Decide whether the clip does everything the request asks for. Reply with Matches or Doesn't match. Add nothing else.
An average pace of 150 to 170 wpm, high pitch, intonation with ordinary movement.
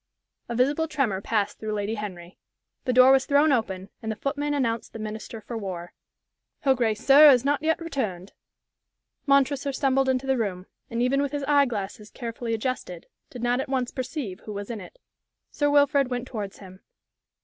Doesn't match